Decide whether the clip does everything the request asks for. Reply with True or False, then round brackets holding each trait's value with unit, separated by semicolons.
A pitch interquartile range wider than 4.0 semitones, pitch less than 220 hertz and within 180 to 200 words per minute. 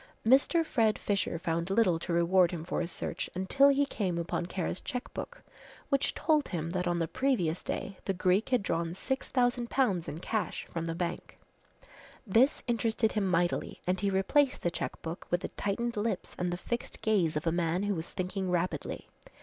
True (5.3 semitones; 190 Hz; 190 wpm)